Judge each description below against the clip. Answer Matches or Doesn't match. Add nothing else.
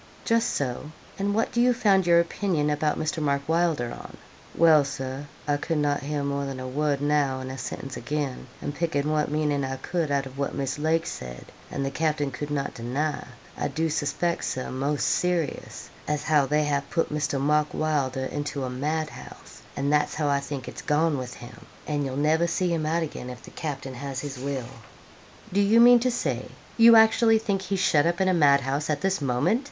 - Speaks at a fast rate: Matches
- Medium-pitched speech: Matches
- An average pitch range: Matches